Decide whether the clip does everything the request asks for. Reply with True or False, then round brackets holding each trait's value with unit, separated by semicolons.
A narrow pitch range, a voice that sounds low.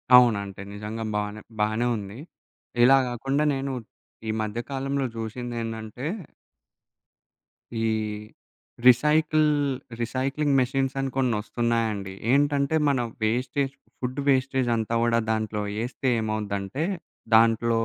False (3.6 semitones; 120 Hz)